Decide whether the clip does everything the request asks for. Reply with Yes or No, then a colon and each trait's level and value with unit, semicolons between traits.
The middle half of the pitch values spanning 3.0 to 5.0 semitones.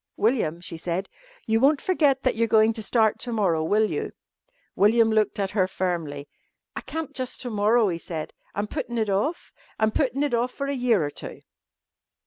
Yes: average, 4.5 semitones